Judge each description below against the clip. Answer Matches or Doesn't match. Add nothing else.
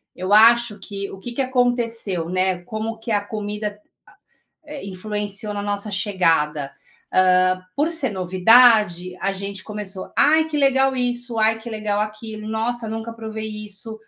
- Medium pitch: Doesn't match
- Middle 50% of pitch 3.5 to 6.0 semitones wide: Doesn't match